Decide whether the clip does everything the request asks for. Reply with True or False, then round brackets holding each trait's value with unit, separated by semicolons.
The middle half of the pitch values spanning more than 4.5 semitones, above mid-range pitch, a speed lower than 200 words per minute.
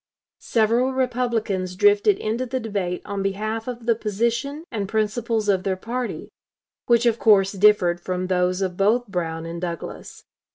False (3.8 semitones; 210 Hz; 155 wpm)